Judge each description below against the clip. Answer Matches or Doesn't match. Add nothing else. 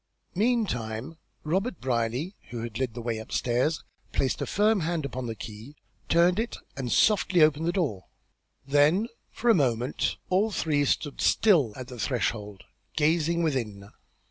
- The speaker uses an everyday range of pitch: Doesn't match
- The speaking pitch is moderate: Matches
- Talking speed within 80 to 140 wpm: Doesn't match